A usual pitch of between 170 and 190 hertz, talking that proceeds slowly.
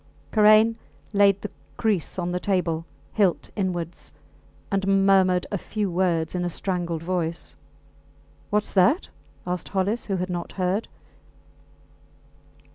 Yes: medium, 185 Hz; slow, 120 wpm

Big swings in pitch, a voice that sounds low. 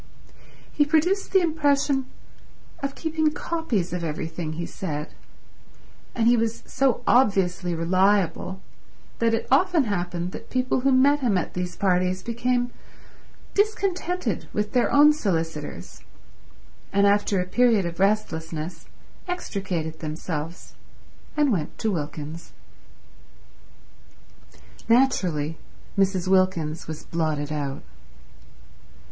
No: wide, 7.7 semitones; high, 195 Hz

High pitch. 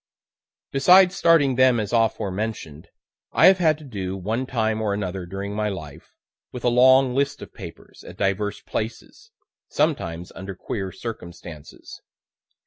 No: low, 110 Hz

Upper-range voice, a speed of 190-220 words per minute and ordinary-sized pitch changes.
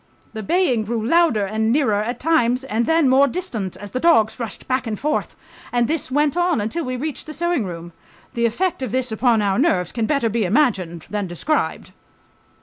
No: high, 240 Hz; average, 200 wpm; wide, 5.9 semitones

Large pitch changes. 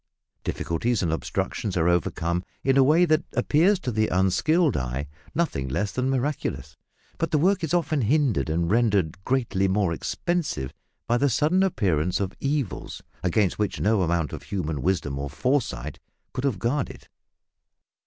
Yes: wide, 9.0 semitones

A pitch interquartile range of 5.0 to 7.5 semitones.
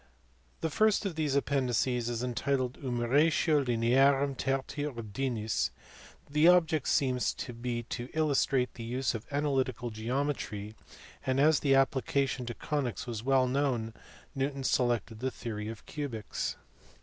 No: average, 3.0 semitones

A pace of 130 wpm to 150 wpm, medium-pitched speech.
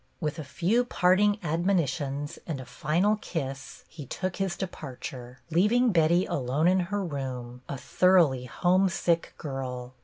Yes: average, 140 wpm; medium, 165 Hz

